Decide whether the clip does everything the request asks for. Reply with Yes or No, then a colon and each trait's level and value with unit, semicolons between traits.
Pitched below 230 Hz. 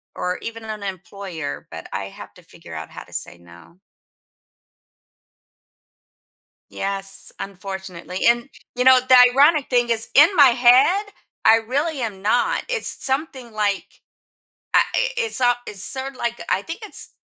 No: high, 235 Hz